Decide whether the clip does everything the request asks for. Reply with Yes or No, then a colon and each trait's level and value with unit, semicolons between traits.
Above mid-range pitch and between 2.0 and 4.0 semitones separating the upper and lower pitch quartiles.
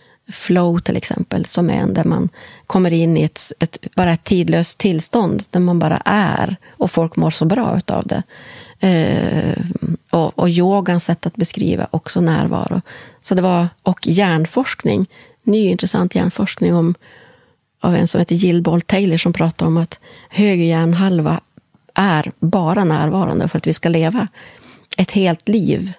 No: medium, 175 Hz; narrow, 2.6 semitones